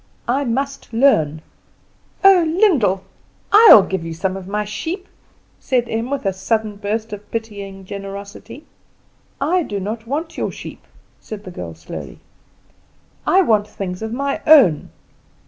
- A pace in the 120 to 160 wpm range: Yes, average, 145 wpm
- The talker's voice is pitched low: No, high, 215 Hz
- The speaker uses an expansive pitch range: Yes, wide, 6.1 semitones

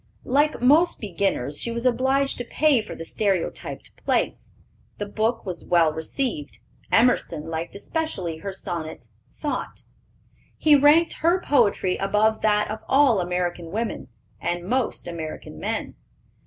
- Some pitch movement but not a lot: No, wide, 7.2 semitones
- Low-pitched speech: No, high, 210 Hz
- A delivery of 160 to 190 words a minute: No, slow, 135 wpm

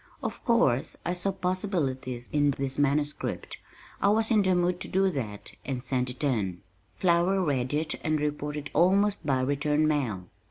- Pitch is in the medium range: Yes, medium, 150 Hz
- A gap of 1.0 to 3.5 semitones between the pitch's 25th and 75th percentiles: No, wide, 5.5 semitones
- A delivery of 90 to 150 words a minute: No, average, 165 wpm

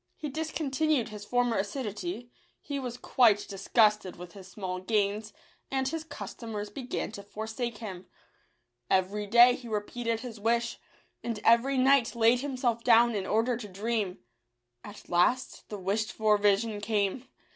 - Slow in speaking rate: No, average, 150 wpm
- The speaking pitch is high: Yes, high, 225 Hz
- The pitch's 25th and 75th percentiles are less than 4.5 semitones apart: Yes, average, 3.2 semitones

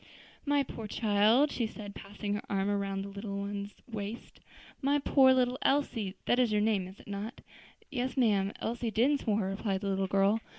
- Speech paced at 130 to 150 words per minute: No, average, 180 wpm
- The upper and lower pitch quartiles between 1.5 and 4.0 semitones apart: Yes, average, 3.6 semitones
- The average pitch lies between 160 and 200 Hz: No, high, 210 Hz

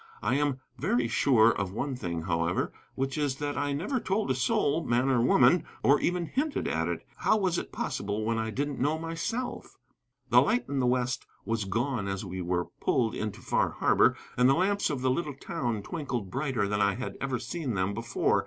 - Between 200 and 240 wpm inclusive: Yes, fast, 205 wpm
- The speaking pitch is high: No, low, 130 Hz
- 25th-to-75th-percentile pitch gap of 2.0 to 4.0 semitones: No, average, 5.1 semitones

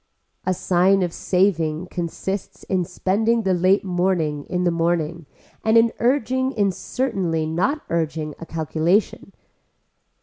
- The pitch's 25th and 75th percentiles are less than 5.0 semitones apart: Yes, average, 3.6 semitones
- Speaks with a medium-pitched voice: Yes, medium, 180 Hz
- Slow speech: Yes, slow, 130 wpm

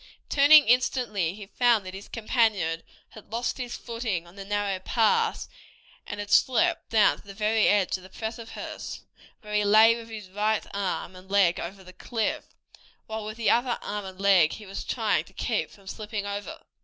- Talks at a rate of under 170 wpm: No, average, 190 wpm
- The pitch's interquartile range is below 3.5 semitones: Yes, average, 2.9 semitones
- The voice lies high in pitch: Yes, high, 210 Hz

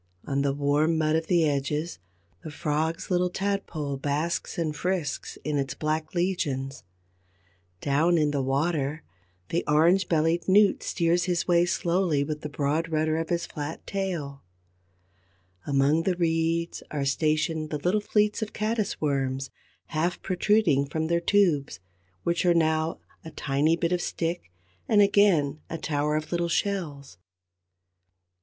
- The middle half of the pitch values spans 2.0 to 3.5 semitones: Yes, average, 3.0 semitones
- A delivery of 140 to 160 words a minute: Yes, average, 150 wpm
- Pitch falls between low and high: Yes, medium, 160 Hz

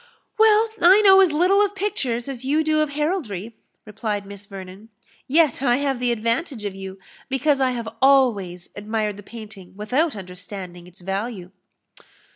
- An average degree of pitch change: No, wide, 6.9 semitones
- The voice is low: No, high, 235 Hz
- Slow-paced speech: No, average, 160 wpm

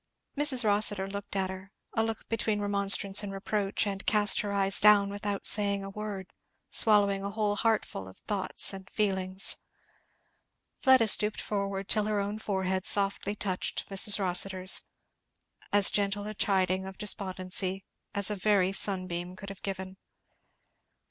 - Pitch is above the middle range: Yes, high, 200 Hz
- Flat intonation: Yes, narrow, 1.5 semitones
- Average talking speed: Yes, average, 150 wpm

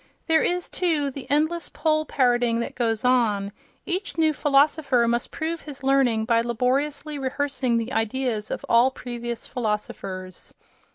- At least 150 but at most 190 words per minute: No, average, 140 wpm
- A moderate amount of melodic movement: Yes, average, 4.1 semitones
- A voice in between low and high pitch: No, very high, 255 Hz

